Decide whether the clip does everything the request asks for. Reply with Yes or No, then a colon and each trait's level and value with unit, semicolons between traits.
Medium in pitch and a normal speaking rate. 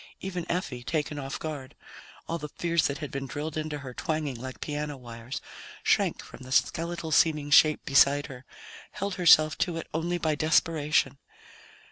Yes: medium, 150 Hz; average, 165 wpm